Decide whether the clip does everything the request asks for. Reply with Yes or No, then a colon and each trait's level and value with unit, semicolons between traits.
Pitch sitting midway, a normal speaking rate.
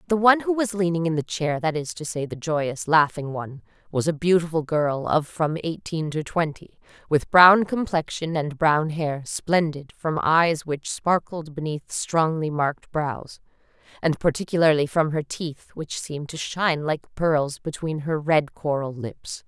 Yes: medium, 160 Hz; average, 165 wpm